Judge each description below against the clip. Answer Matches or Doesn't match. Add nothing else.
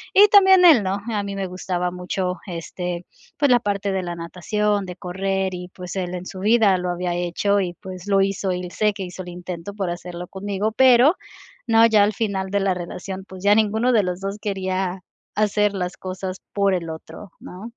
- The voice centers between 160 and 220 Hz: Matches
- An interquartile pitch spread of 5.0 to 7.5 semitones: Doesn't match